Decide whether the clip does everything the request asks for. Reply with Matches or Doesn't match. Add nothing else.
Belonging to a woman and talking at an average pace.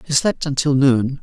Doesn't match